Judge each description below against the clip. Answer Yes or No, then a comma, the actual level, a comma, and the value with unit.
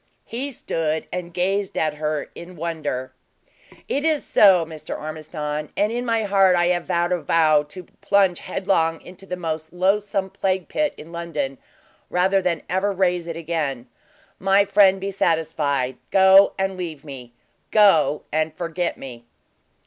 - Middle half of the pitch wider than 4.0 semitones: No, average, 3.7 semitones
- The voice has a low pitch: No, medium, 175 Hz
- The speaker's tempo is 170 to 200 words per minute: No, average, 155 wpm